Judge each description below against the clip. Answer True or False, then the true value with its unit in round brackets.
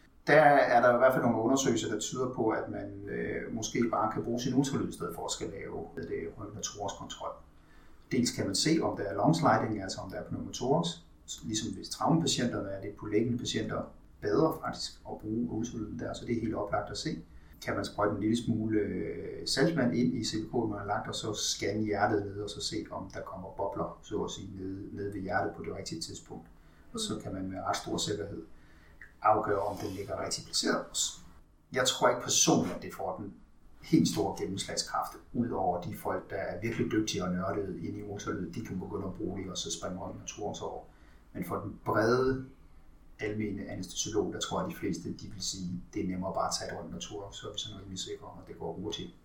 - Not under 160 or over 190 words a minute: False (225 wpm)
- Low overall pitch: True (100 Hz)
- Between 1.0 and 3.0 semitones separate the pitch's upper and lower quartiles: True (2.4 semitones)